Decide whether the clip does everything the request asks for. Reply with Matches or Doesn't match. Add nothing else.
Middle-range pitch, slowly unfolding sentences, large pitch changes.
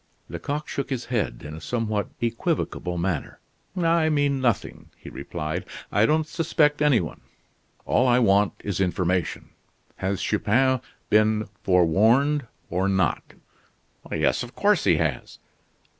Doesn't match